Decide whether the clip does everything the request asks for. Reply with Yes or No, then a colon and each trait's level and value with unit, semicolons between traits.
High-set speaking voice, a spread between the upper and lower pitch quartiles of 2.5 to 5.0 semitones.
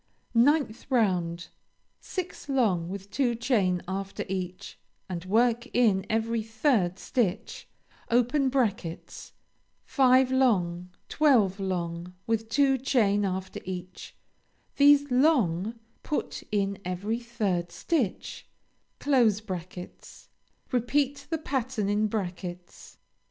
No: high, 215 Hz; wide, 5.5 semitones